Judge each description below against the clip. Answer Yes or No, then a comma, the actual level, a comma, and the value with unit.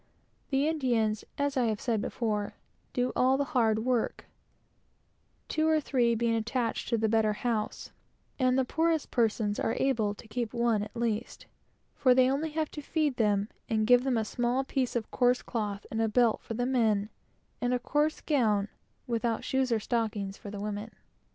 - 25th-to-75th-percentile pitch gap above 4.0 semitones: No, average, 3.0 semitones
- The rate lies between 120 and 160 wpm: No, average, 180 wpm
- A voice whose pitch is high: Yes, high, 235 Hz